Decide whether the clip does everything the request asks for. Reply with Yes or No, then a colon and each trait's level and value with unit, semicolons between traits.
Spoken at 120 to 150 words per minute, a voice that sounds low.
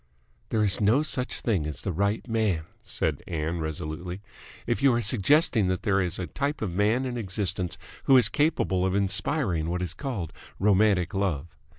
No: average, 180 wpm; low, 100 Hz